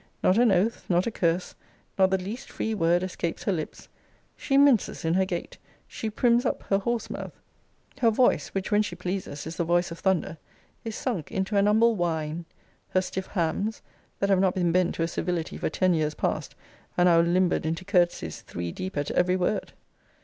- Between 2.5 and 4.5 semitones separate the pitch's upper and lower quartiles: Yes, average, 3.3 semitones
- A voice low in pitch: No, medium, 185 Hz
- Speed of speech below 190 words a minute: No, average, 200 wpm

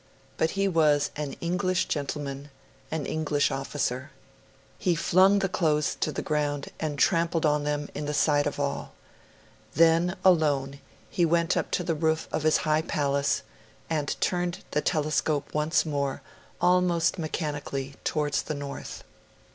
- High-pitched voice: No, medium, 155 Hz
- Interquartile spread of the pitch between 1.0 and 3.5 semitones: Yes, narrow, 2.5 semitones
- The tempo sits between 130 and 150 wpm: Yes, average, 145 wpm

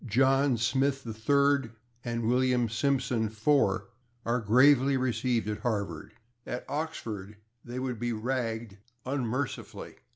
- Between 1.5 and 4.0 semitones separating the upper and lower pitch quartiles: Yes, average, 3.1 semitones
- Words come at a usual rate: No, slow, 110 wpm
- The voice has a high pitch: No, low, 120 Hz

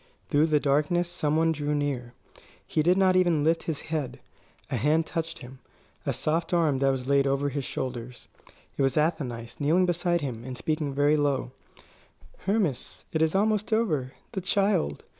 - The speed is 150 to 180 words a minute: Yes, average, 170 wpm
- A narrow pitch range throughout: No, average, 3.8 semitones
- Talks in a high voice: No, medium, 150 Hz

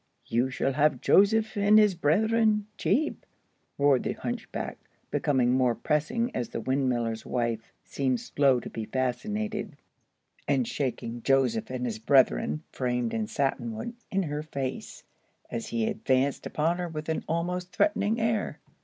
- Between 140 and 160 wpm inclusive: Yes, average, 145 wpm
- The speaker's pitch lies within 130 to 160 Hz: Yes, medium, 140 Hz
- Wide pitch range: Yes, wide, 8.0 semitones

